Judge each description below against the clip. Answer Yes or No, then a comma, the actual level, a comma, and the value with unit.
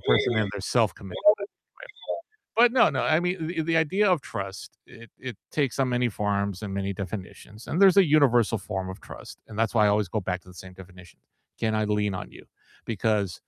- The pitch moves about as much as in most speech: No, wide, 6.6 semitones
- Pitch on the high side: No, low, 110 Hz